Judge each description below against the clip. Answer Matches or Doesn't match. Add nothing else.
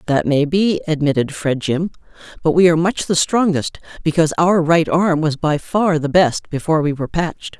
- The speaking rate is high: Doesn't match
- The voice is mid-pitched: Matches